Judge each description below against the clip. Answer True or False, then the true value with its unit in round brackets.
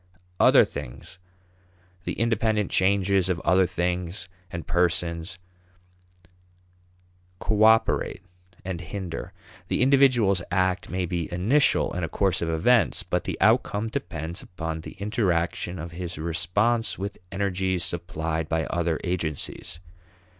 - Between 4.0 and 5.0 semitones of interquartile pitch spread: False (3.2 semitones)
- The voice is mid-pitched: False (90 Hz)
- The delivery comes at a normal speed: False (120 wpm)